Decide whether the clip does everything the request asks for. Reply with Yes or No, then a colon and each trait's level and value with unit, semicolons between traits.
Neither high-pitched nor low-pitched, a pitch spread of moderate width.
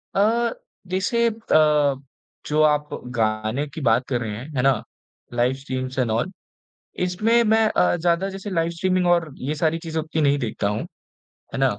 No: medium, 155 Hz; wide, 6.3 semitones